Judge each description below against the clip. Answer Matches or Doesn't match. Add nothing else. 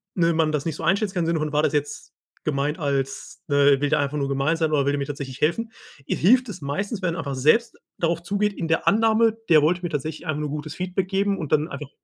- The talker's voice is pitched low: Doesn't match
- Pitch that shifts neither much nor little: Matches